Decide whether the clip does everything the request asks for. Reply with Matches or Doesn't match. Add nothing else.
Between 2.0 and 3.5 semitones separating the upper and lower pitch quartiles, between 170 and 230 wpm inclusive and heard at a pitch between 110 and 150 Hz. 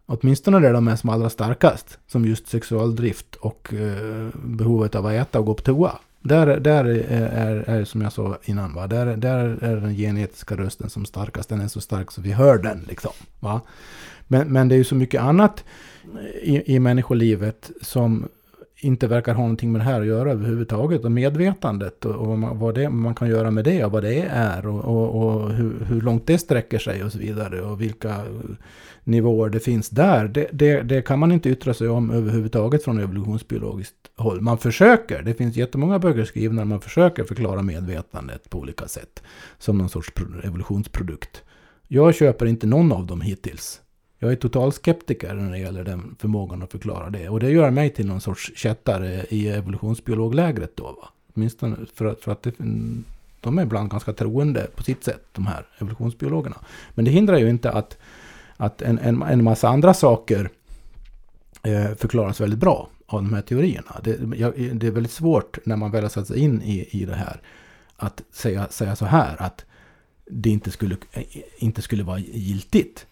Matches